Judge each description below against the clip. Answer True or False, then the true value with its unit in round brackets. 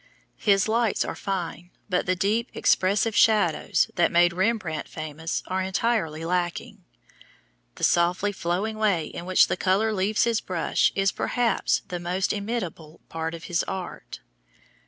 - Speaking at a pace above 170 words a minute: False (145 wpm)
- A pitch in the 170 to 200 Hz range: True (185 Hz)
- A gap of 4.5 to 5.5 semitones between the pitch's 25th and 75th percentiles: False (3.5 semitones)